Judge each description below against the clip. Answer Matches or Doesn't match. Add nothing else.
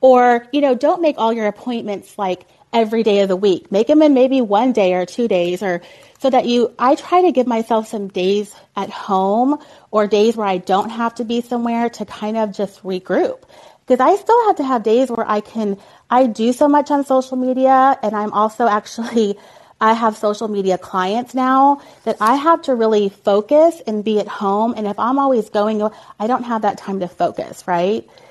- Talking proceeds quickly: Matches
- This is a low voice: Doesn't match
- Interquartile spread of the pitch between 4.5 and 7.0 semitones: Doesn't match